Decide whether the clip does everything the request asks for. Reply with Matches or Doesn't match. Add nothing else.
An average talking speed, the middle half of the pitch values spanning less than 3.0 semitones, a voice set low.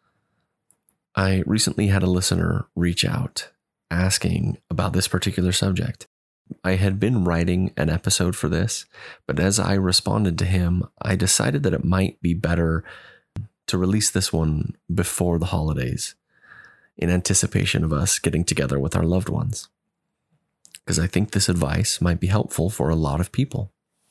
Matches